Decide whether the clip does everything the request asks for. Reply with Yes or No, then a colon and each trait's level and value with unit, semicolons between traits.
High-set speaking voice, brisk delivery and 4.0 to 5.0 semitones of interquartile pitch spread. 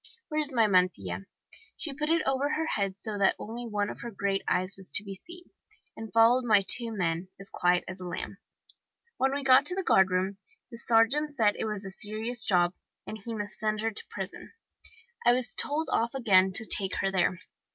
Yes: high, 215 Hz; fast, 210 wpm; average, 4.4 semitones